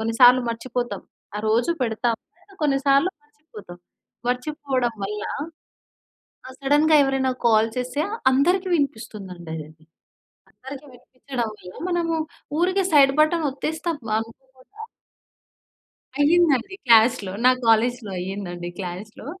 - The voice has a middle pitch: No, very high, 255 Hz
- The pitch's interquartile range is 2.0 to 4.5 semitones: No, average, 5.1 semitones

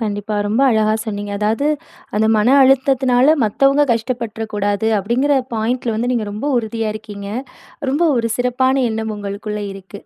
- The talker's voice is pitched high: Yes, high, 220 Hz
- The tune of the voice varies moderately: Yes, average, 3.1 semitones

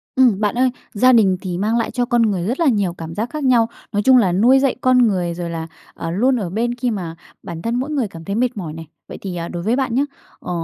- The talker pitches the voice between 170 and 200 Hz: No, high, 220 Hz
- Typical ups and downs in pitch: No, wide, 5.7 semitones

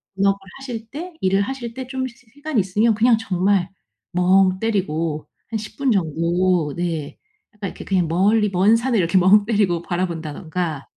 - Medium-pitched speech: No, high, 195 Hz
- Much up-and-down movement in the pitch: No, average, 4.4 semitones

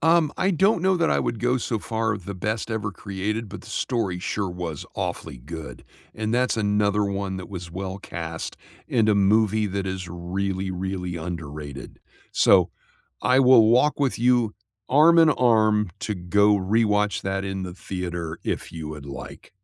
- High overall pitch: No, low, 100 Hz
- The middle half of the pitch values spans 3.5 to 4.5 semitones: Yes, average, 3.9 semitones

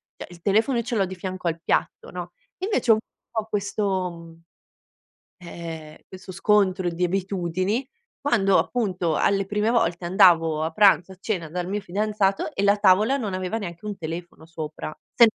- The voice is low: No, high, 190 Hz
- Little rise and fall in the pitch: No, average, 3.3 semitones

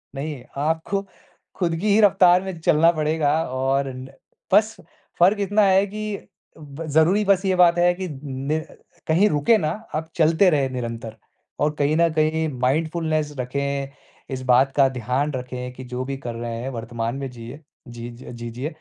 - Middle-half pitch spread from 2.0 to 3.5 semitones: No, average, 4.8 semitones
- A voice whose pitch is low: No, medium, 150 Hz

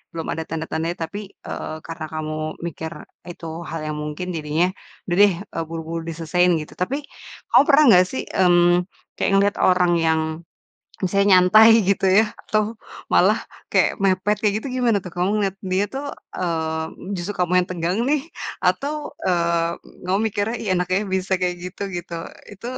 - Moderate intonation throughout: Yes, average, 3.2 semitones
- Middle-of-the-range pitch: Yes, medium, 180 Hz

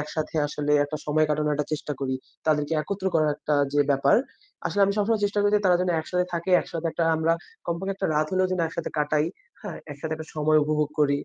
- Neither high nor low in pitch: Yes, medium, 155 Hz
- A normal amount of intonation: Yes, average, 3.3 semitones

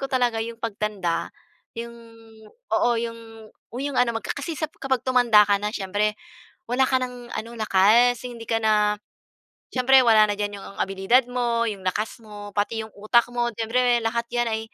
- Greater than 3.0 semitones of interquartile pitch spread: No, average, 2.7 semitones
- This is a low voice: No, high, 230 Hz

